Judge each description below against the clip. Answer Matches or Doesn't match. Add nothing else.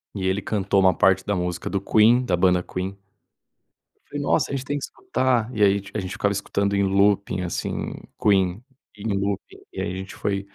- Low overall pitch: Matches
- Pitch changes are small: Matches